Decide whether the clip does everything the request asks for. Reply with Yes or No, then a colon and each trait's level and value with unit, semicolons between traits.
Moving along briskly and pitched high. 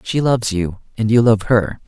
No: fast, 225 wpm; low, 110 Hz